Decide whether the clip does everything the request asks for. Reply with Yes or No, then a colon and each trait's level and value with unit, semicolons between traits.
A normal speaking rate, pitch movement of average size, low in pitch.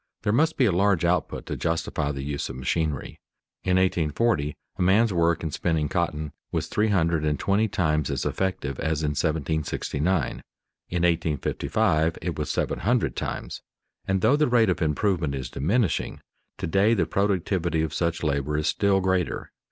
Yes: average, 170 wpm; average, 4.1 semitones; very low, 85 Hz